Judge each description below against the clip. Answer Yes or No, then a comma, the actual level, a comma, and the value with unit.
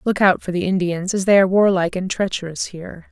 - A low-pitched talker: No, medium, 185 Hz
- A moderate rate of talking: No, fast, 230 wpm